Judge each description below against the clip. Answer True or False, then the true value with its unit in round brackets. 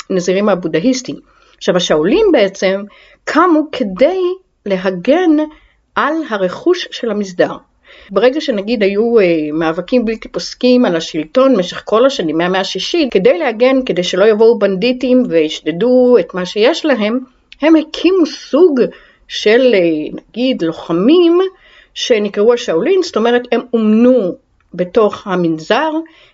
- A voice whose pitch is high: True (240 Hz)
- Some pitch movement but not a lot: False (7.8 semitones)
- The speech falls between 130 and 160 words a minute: False (115 wpm)